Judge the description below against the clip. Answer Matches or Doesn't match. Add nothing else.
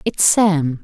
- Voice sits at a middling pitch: Matches